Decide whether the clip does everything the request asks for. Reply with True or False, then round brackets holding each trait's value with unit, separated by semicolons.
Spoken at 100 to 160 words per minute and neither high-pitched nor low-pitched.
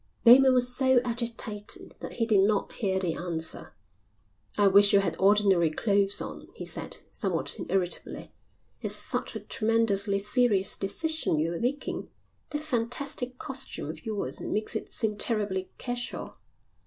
False (140 wpm; 210 Hz)